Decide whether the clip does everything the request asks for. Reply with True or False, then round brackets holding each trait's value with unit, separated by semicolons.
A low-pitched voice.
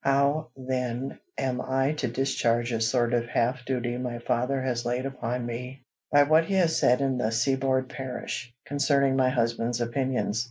True (125 Hz)